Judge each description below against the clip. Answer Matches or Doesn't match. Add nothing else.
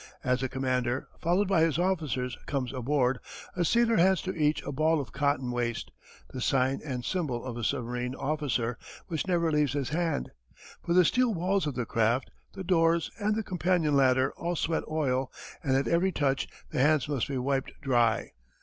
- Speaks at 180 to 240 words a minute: Matches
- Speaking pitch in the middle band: Matches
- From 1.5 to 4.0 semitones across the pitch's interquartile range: Doesn't match